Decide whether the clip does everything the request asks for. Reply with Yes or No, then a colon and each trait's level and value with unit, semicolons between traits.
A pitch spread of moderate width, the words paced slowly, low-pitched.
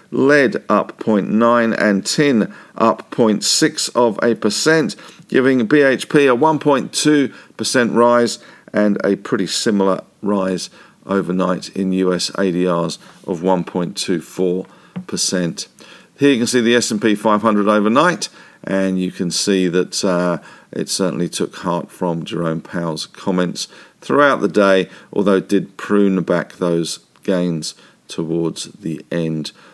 Yes: average, 4.2 semitones; slow, 125 wpm; very low, 95 Hz